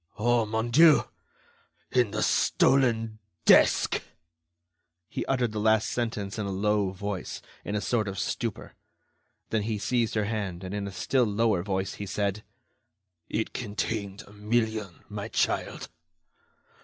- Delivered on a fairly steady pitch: Yes, narrow, 2.1 semitones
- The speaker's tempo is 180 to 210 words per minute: No, average, 145 wpm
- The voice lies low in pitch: Yes, low, 105 Hz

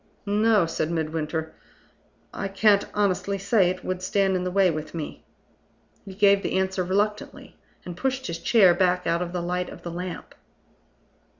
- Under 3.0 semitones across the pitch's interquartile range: Yes, narrow, 2.5 semitones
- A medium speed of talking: Yes, average, 170 wpm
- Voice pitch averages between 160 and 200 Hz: Yes, medium, 185 Hz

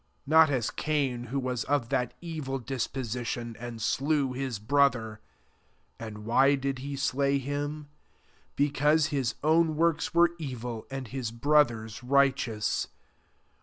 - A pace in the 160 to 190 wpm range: No, slow, 135 wpm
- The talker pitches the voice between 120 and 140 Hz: Yes, low, 135 Hz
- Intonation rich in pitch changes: No, average, 3.3 semitones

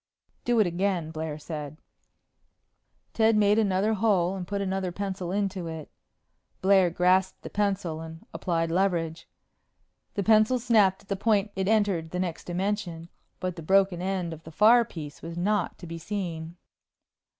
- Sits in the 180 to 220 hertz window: Yes, medium, 185 Hz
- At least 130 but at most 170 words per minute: Yes, average, 160 wpm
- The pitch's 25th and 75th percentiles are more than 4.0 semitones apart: No, average, 3.3 semitones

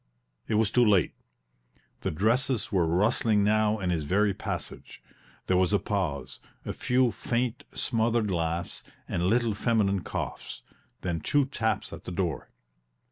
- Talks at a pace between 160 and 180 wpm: No, average, 145 wpm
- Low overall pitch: Yes, low, 105 Hz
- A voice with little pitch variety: No, average, 4.2 semitones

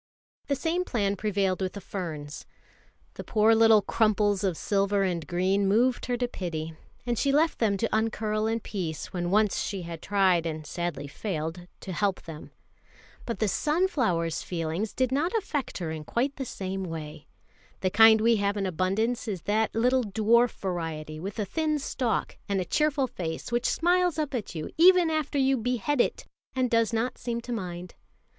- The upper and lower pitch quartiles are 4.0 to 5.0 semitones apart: No, wide, 5.4 semitones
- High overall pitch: Yes, high, 210 Hz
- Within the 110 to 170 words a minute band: No, average, 180 wpm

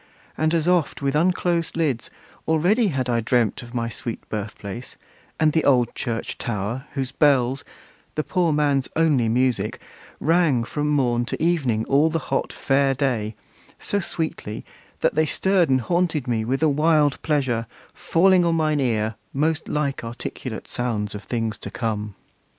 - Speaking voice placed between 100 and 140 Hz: Yes, low, 135 Hz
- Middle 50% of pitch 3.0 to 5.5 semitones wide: Yes, average, 5.1 semitones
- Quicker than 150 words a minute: Yes, average, 160 wpm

